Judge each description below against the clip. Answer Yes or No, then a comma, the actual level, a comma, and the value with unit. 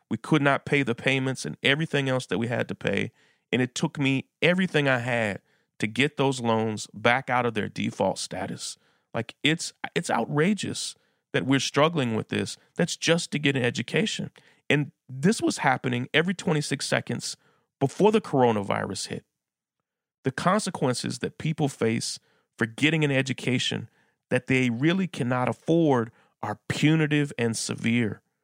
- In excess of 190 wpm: No, average, 160 wpm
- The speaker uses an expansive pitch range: No, average, 4.0 semitones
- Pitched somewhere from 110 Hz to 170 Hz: Yes, low, 135 Hz